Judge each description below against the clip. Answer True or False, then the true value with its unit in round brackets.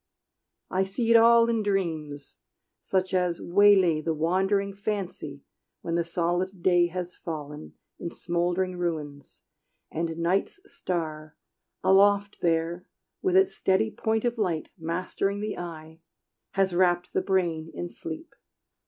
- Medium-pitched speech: True (180 Hz)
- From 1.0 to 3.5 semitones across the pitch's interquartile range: True (3.1 semitones)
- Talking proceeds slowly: True (130 wpm)